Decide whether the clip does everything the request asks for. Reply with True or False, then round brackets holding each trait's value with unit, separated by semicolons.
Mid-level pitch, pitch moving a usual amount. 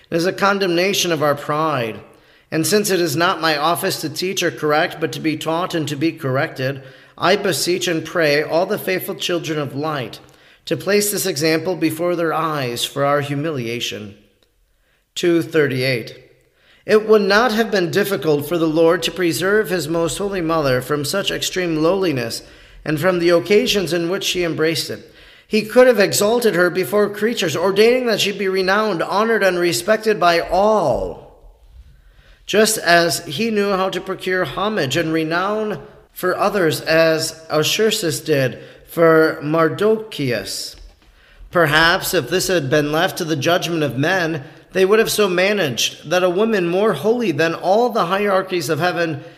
True (170 Hz; 3.6 semitones)